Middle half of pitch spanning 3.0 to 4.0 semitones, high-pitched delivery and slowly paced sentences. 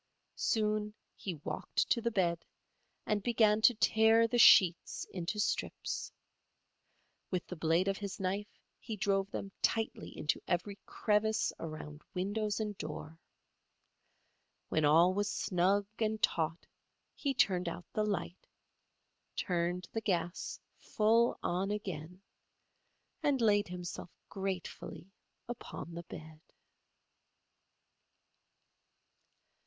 Yes: average, 3.6 semitones; high, 195 Hz; slow, 110 wpm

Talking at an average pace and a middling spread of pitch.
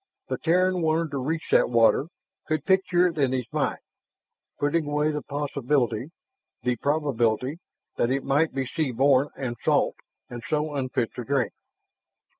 Yes: average, 155 wpm; average, 3.5 semitones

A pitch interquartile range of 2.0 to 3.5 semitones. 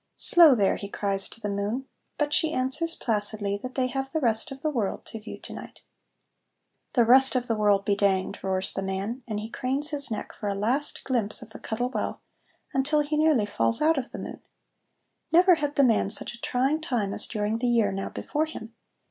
No: average, 5.2 semitones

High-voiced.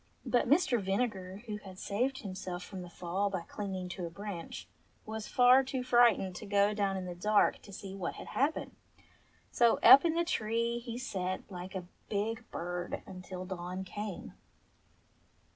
Yes: high, 200 Hz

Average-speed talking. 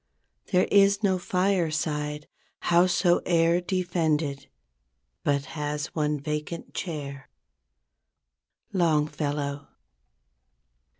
No: slow, 65 wpm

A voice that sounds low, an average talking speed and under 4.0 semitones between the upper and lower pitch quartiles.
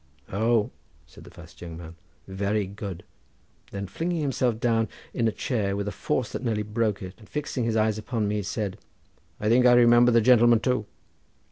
Yes: low, 110 Hz; average, 190 wpm; average, 2.9 semitones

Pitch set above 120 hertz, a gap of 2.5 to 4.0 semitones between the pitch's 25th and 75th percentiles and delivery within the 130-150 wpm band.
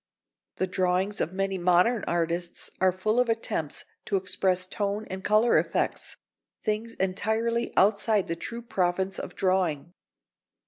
Yes: high, 190 Hz; average, 3.0 semitones; slow, 135 wpm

